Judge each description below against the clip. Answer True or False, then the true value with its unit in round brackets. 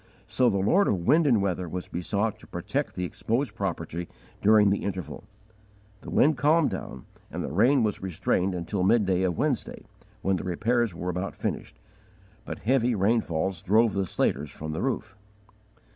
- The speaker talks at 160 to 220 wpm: True (170 wpm)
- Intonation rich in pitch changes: False (4.4 semitones)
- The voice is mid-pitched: False (100 Hz)